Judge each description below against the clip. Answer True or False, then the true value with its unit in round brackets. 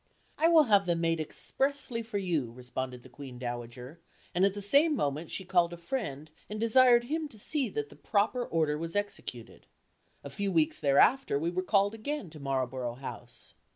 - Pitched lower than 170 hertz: False (175 Hz)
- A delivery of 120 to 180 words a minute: False (190 wpm)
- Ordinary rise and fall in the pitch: False (8.1 semitones)